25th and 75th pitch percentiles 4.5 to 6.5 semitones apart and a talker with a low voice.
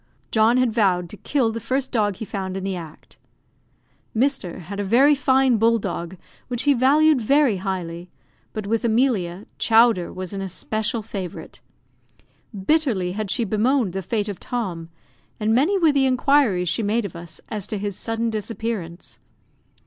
No: average, 4.8 semitones; high, 215 Hz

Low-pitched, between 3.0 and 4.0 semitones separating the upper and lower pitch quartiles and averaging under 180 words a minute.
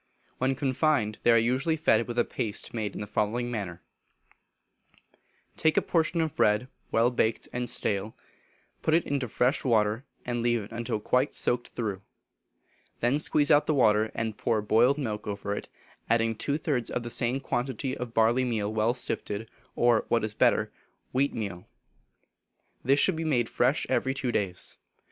Yes: low, 120 Hz; average, 3.4 semitones; average, 170 wpm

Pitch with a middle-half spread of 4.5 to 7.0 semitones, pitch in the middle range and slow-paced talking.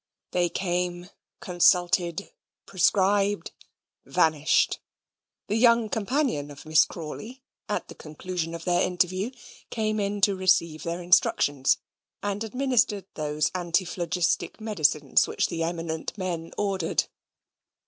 No: average, 3.6 semitones; medium, 180 Hz; slow, 110 wpm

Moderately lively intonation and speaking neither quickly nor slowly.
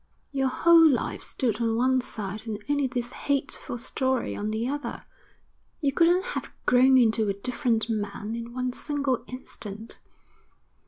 Yes: average, 3.3 semitones; average, 150 wpm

